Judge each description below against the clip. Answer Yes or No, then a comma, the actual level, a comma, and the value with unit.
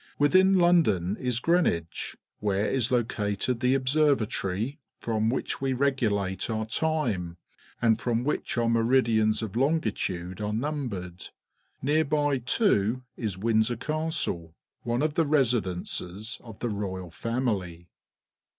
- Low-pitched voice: Yes, low, 115 Hz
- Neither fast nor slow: No, slow, 125 wpm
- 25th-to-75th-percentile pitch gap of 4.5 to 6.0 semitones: Yes, average, 5.2 semitones